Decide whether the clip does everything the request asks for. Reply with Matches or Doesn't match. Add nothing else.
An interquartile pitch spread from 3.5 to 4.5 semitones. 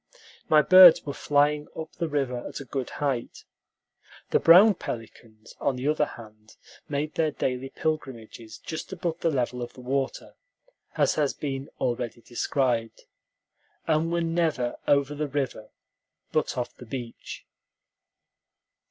Matches